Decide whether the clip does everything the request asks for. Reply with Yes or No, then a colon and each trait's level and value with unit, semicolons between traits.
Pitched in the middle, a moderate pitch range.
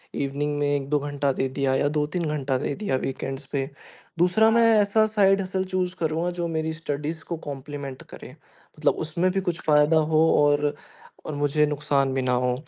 Yes: medium, 150 Hz; average, 3.4 semitones